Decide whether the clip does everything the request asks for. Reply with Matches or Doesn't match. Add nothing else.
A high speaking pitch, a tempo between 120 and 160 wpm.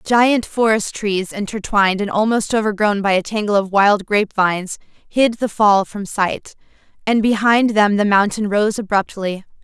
Matches